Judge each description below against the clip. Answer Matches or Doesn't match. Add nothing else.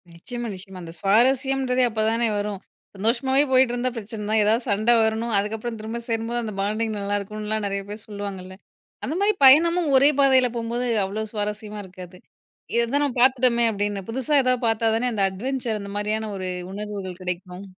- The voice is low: Doesn't match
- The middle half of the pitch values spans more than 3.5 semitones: Doesn't match